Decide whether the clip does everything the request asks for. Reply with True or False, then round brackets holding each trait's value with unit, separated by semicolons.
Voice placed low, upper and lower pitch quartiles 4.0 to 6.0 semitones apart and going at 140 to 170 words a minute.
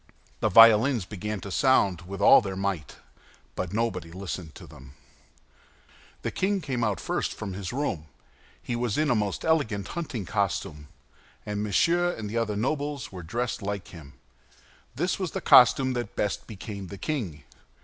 True (105 Hz; 4.7 semitones; 165 wpm)